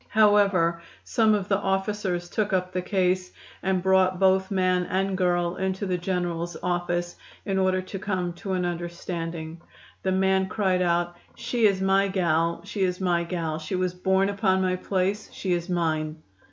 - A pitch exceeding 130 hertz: Yes, medium, 185 Hz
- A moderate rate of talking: Yes, average, 170 wpm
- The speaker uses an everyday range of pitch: No, narrow, 1.6 semitones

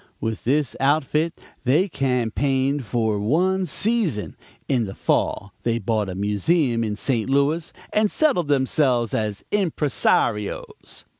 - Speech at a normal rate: No, slow, 125 wpm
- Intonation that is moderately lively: No, wide, 5.9 semitones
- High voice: No, low, 130 Hz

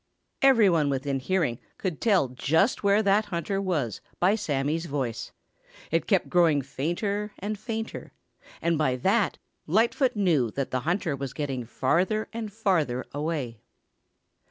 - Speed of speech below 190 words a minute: Yes, average, 140 wpm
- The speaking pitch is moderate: Yes, medium, 170 Hz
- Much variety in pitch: Yes, wide, 6.7 semitones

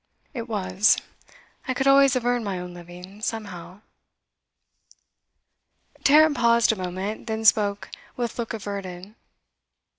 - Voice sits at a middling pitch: No, high, 215 Hz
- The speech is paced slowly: Yes, slow, 120 wpm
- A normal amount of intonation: Yes, average, 4.2 semitones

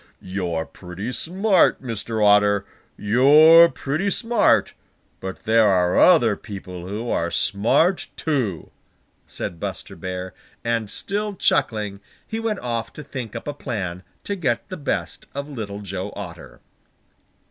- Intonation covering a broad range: Yes, wide, 7.3 semitones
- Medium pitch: No, low, 115 Hz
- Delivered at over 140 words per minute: No, slow, 135 wpm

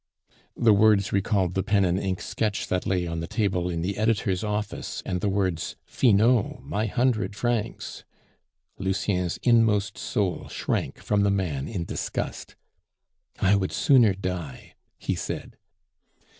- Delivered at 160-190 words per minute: No, average, 145 wpm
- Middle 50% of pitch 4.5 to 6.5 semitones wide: No, average, 2.8 semitones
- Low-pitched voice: Yes, low, 100 Hz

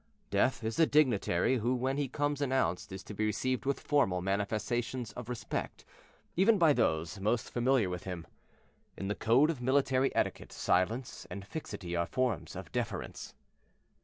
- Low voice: Yes, low, 120 Hz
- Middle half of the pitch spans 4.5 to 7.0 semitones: Yes, wide, 5.4 semitones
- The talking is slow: No, average, 160 wpm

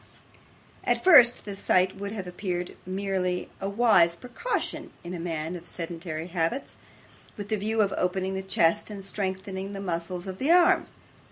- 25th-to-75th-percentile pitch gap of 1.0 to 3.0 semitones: Yes, narrow, 2.4 semitones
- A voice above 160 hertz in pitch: Yes, high, 190 Hz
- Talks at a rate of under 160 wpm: No, average, 165 wpm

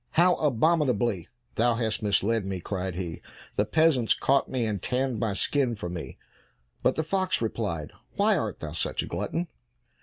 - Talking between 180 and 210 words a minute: No, average, 170 wpm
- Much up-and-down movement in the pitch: Yes, wide, 5.9 semitones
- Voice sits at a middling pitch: No, low, 115 Hz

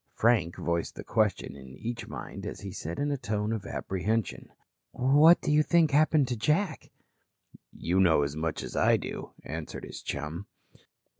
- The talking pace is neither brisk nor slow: Yes, average, 170 wpm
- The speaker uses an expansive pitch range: Yes, wide, 9.0 semitones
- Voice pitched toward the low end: Yes, low, 110 Hz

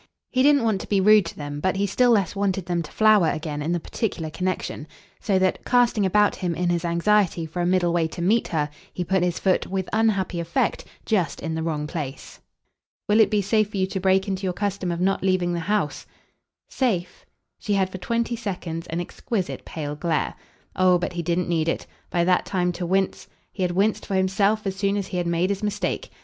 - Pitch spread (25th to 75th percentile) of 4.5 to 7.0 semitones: No, average, 3.0 semitones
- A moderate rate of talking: No, fast, 225 wpm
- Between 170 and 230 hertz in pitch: Yes, medium, 185 Hz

